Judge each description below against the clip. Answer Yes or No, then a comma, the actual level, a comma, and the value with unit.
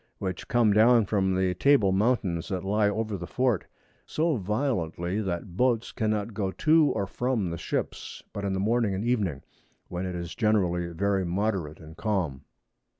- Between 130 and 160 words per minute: No, average, 175 wpm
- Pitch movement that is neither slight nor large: Yes, average, 3.7 semitones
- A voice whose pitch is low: Yes, low, 100 Hz